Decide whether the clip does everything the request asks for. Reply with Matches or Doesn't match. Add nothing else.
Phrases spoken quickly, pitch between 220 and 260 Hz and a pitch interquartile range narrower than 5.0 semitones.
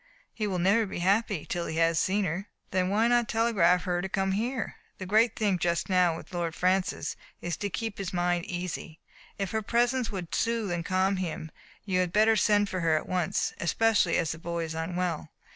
Doesn't match